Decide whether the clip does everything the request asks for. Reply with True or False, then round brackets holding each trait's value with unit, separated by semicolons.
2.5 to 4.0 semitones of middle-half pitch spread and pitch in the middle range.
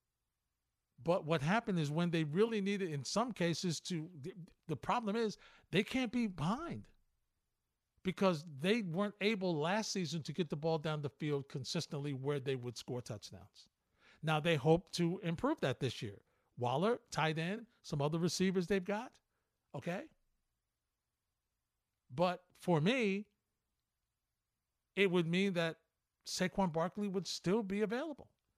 False (4.6 semitones; 175 Hz)